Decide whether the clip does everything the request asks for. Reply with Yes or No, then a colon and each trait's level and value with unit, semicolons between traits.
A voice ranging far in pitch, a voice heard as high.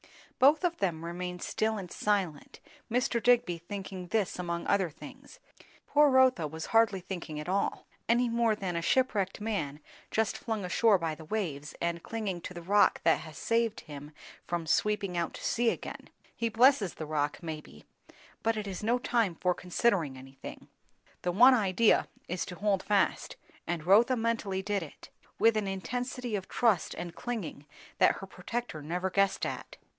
No: average, 4.9 semitones; high, 195 Hz